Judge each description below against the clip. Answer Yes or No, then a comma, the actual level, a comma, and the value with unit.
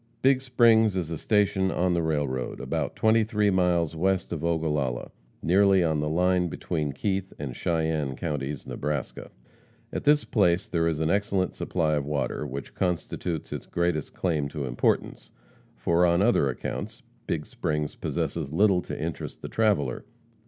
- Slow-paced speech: No, average, 160 wpm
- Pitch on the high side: No, very low, 85 Hz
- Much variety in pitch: No, average, 4.2 semitones